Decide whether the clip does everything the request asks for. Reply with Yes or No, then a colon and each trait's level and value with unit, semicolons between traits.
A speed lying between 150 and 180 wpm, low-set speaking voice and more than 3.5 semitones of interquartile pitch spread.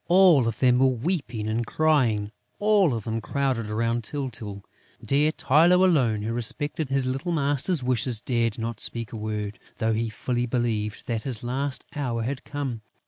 Yes: average, 170 wpm; low, 125 Hz; average, 4.0 semitones